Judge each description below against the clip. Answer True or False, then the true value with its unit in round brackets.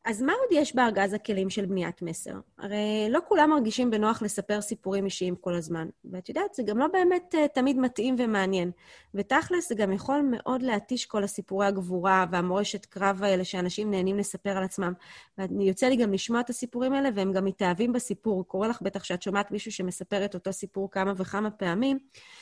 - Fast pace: True (185 wpm)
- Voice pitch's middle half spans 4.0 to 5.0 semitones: True (4.4 semitones)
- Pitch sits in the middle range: False (205 Hz)